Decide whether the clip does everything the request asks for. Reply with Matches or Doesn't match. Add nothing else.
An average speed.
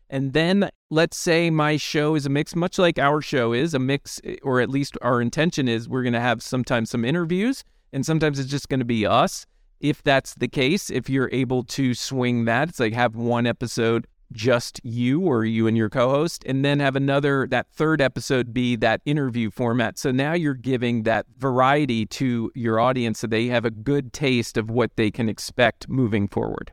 Doesn't match